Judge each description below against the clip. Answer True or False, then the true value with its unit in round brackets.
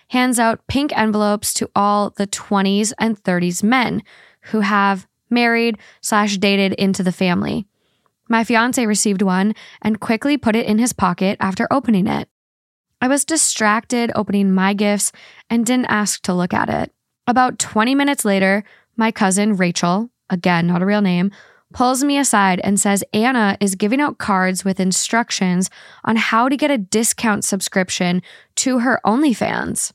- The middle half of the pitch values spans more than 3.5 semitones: False (3.1 semitones)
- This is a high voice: True (210 Hz)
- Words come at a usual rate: True (160 wpm)